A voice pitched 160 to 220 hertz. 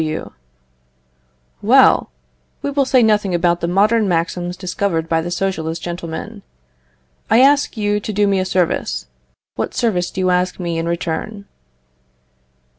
Yes: medium, 185 Hz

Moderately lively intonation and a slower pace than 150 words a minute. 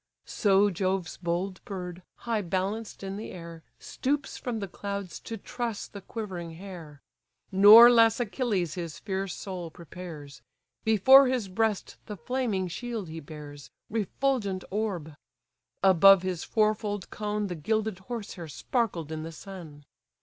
Yes: average, 4.1 semitones; average, 140 wpm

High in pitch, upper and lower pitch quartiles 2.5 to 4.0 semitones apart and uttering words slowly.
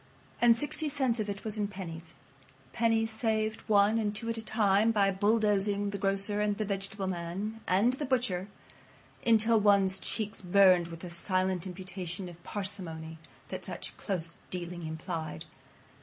No: high, 200 Hz; average, 3.0 semitones; average, 155 wpm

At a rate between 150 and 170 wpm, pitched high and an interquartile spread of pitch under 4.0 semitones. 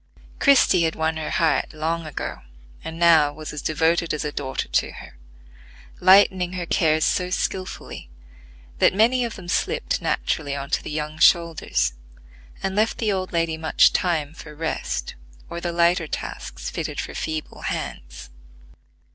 No: average, 155 wpm; medium, 165 Hz; average, 2.8 semitones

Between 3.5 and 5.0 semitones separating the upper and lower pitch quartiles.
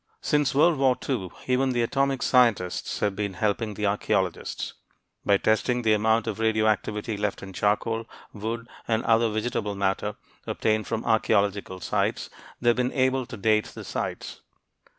No: average, 2.9 semitones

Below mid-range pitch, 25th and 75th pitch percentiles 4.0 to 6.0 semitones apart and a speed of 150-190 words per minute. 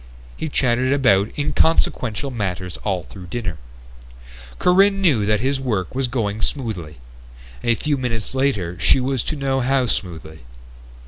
No: low, 120 Hz; wide, 5.5 semitones; average, 140 wpm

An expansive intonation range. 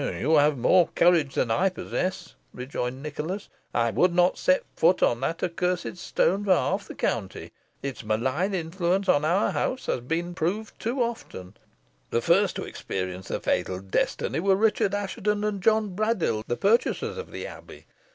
Yes: wide, 6.9 semitones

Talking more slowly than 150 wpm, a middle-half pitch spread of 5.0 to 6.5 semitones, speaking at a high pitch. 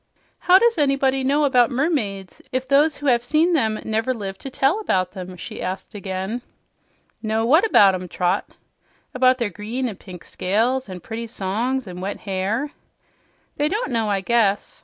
No: average, 175 wpm; wide, 5.5 semitones; high, 230 Hz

